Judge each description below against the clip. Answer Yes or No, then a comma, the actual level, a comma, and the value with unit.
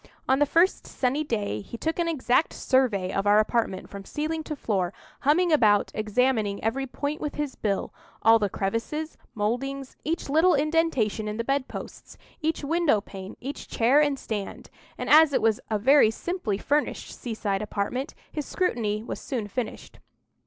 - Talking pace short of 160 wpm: No, average, 165 wpm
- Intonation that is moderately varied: No, wide, 5.9 semitones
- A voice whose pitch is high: Yes, very high, 250 Hz